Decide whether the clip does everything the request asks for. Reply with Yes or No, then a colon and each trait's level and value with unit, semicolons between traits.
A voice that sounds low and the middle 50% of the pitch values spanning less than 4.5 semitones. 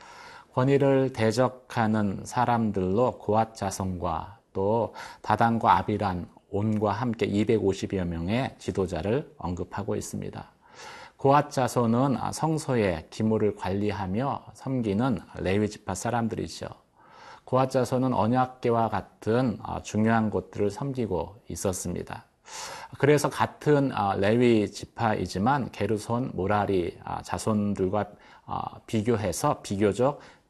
Yes: low, 110 Hz; average, 3.9 semitones